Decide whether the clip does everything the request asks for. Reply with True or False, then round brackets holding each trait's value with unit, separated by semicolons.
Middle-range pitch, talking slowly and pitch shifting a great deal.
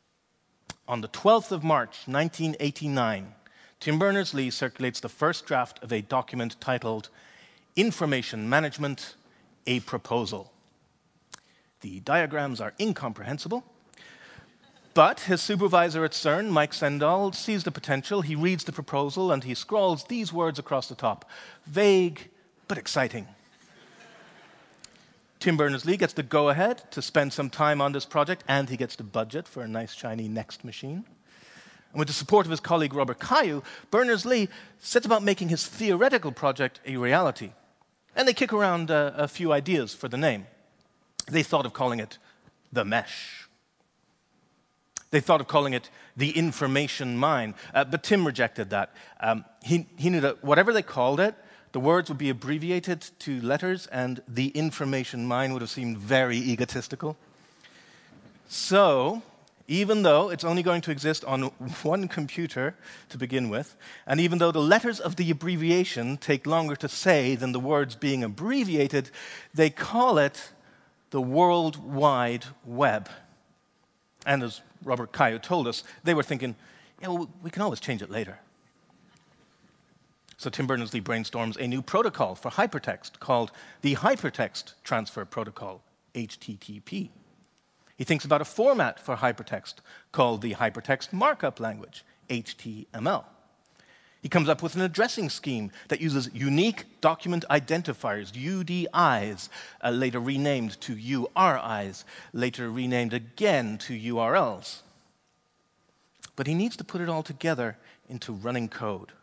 False (145 Hz; 145 wpm; 5.7 semitones)